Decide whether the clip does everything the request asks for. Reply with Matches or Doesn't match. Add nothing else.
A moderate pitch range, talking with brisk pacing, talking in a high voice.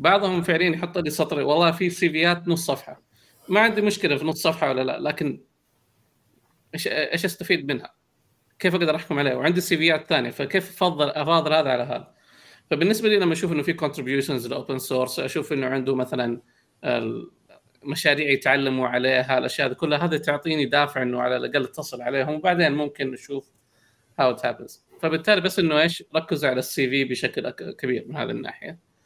Doesn't match